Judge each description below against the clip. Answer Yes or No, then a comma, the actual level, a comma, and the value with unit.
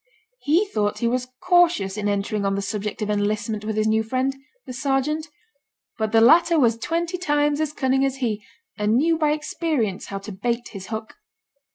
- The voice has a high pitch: Yes, high, 235 Hz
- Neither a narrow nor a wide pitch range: No, wide, 6.0 semitones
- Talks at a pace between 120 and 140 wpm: No, average, 190 wpm